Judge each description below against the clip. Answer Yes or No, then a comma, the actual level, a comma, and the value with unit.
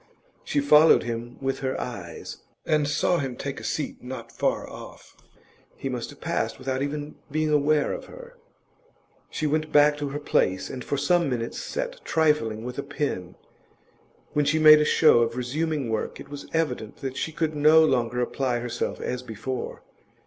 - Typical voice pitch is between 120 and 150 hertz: Yes, medium, 140 Hz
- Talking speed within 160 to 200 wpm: Yes, average, 180 wpm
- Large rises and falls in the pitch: No, average, 3.7 semitones